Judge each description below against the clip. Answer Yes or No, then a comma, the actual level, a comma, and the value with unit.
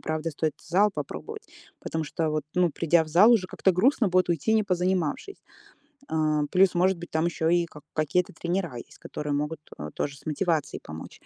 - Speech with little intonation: No, average, 3.1 semitones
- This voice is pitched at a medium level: Yes, medium, 170 Hz